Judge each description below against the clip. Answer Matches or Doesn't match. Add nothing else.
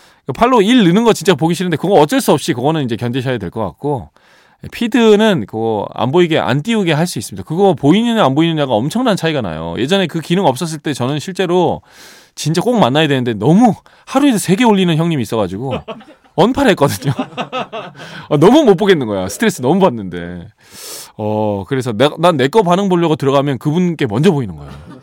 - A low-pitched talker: Doesn't match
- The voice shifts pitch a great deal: Matches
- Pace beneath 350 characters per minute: Doesn't match